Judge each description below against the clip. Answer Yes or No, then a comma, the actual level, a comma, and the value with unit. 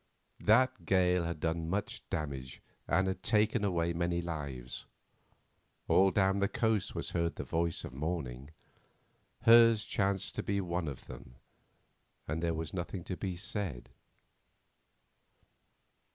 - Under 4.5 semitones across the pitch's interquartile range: Yes, average, 3.4 semitones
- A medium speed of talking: No, slow, 125 wpm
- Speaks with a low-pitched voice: Yes, very low, 90 Hz